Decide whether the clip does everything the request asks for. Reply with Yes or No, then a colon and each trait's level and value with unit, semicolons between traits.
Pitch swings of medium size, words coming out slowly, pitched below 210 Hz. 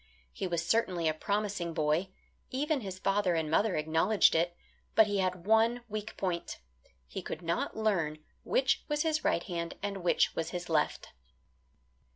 No: average, 4.3 semitones; average, 165 wpm; medium, 185 Hz